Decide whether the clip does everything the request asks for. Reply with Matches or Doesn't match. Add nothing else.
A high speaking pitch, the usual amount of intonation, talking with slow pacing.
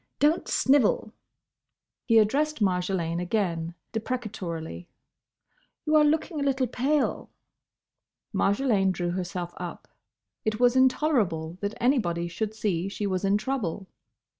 Doesn't match